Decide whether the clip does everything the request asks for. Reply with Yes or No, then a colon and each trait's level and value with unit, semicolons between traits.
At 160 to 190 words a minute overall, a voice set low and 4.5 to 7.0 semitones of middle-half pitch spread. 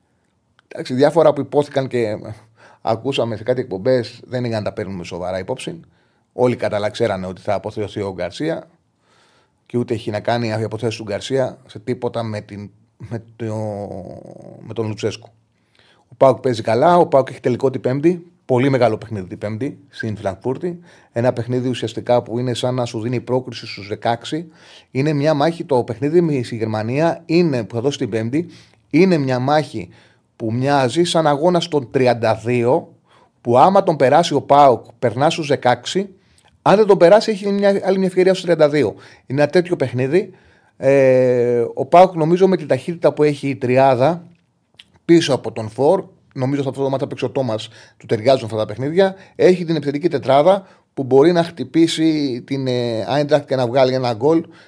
Yes: fast, 170 wpm; low, 130 Hz; average, 5.2 semitones